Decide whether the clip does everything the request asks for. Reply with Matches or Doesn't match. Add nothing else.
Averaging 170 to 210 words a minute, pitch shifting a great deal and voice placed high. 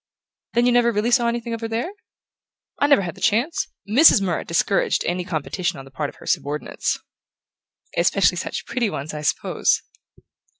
Matches